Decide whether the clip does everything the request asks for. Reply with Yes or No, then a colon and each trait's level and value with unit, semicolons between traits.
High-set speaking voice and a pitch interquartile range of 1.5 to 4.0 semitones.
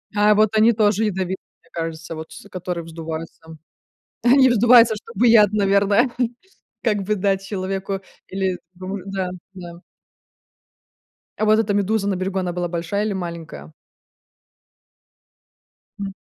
Yes: high, 195 Hz; average, 2.9 semitones